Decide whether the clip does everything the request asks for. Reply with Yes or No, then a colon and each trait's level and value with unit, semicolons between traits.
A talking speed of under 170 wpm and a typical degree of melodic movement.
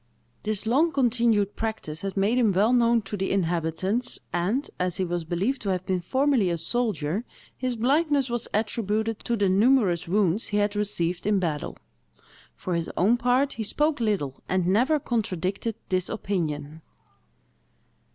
Yes: average, 160 wpm; average, 4.7 semitones